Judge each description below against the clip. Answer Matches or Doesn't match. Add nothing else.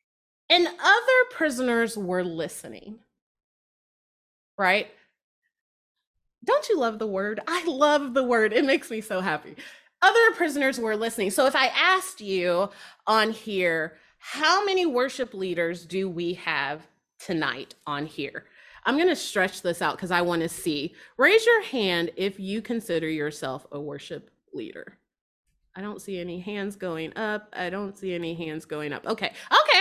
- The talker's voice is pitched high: Matches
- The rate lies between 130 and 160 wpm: Matches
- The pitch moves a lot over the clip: Matches